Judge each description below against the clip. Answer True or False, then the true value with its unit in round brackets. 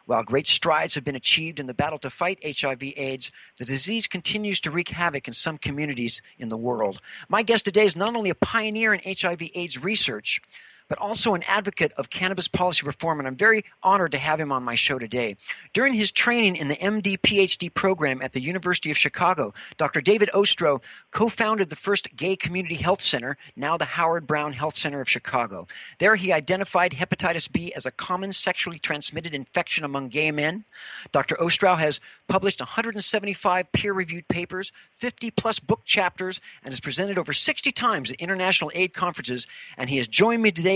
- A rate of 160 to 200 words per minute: True (190 wpm)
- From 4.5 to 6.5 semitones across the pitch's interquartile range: True (5.1 semitones)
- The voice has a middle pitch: True (175 Hz)